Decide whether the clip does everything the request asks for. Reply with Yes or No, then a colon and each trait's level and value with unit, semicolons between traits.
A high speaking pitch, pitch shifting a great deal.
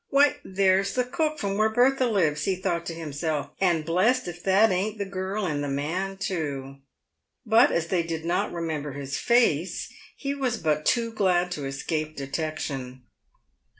No: medium, 180 Hz; wide, 5.7 semitones